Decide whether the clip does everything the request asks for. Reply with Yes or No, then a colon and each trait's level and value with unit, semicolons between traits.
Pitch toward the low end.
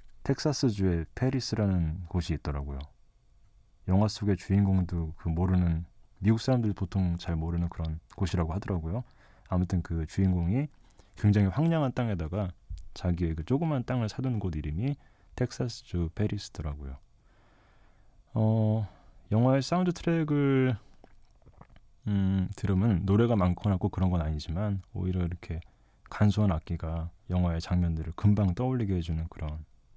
Yes: very low, 95 Hz